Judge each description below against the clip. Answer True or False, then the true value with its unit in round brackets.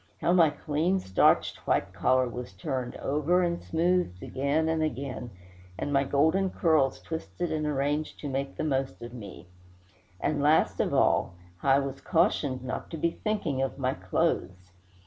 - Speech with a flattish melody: False (3.8 semitones)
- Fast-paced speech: False (165 wpm)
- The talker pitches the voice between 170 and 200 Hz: False (140 Hz)